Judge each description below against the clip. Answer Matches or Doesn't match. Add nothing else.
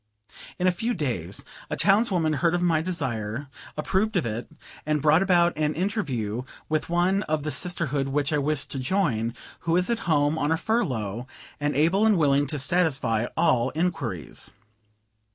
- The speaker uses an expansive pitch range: Doesn't match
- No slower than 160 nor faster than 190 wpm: Matches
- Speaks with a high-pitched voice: Doesn't match